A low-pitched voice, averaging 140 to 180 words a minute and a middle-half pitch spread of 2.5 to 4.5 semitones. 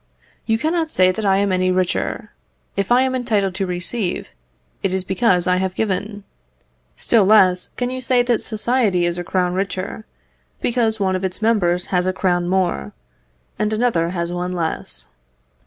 No: high, 190 Hz; average, 170 wpm; average, 3.5 semitones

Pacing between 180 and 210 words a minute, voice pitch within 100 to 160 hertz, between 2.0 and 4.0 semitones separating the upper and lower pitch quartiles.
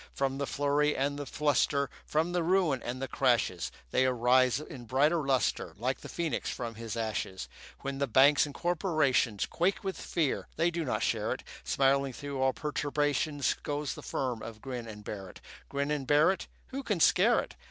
Yes: average, 185 wpm; medium, 140 Hz; average, 2.9 semitones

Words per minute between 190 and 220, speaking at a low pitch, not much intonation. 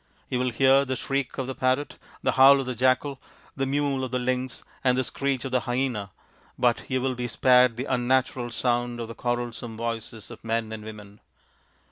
Yes: average, 200 wpm; low, 125 Hz; narrow, 1.8 semitones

